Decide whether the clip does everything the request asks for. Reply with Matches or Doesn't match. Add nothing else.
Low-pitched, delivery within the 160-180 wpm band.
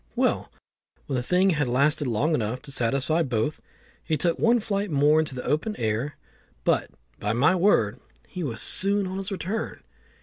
Doesn't match